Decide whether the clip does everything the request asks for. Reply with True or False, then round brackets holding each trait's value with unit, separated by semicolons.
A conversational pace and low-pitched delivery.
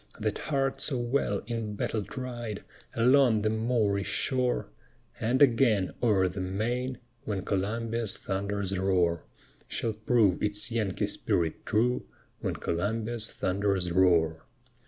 False (120 wpm; 110 Hz)